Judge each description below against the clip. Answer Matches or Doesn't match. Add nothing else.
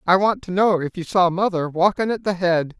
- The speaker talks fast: Matches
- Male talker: Matches